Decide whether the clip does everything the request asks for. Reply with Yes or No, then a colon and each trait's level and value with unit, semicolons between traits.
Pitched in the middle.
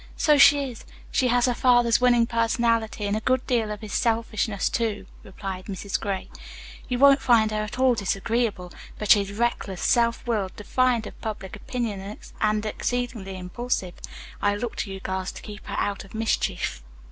No: high, 220 Hz